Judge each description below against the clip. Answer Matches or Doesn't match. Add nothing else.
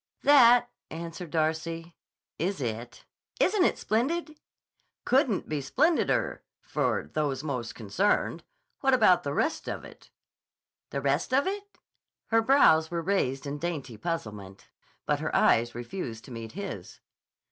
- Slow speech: Matches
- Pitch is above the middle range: Doesn't match